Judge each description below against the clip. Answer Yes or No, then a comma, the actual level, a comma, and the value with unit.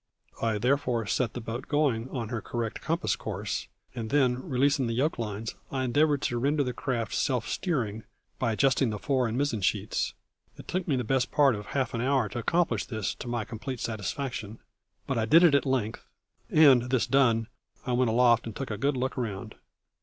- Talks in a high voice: No, low, 125 Hz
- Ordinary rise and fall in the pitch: Yes, average, 3.4 semitones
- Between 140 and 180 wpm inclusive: No, average, 200 wpm